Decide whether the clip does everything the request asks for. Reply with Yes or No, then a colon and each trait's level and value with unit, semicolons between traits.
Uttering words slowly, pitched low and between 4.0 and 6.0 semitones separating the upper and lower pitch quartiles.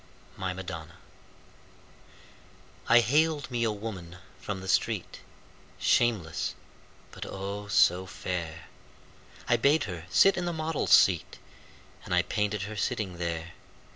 Yes: slow, 125 wpm; low, 100 Hz; average, 5.1 semitones